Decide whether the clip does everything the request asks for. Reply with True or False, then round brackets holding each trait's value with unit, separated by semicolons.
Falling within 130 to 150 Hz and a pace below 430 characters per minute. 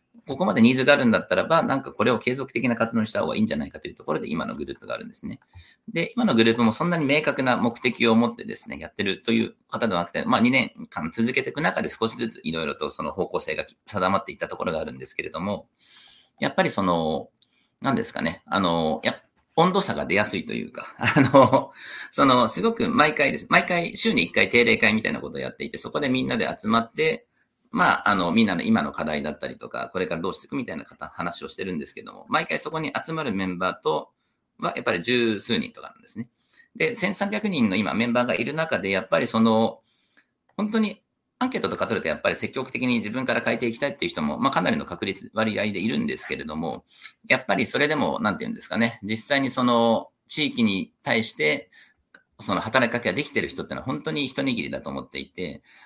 False (135 Hz; 450 characters per minute)